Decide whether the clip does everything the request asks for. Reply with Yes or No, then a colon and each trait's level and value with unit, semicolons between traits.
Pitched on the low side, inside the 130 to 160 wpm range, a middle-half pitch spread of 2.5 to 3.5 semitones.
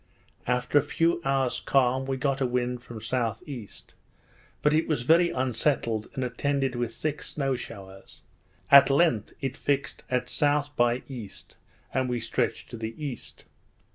Yes: low, 130 Hz; average, 155 wpm; average, 2.8 semitones